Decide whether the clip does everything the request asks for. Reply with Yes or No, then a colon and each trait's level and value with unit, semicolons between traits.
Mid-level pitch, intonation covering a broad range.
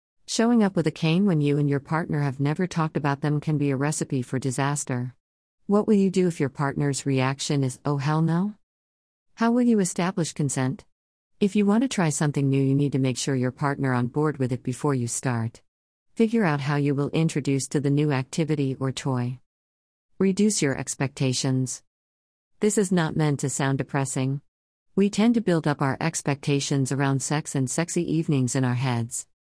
No: medium, 145 Hz; average, 3.8 semitones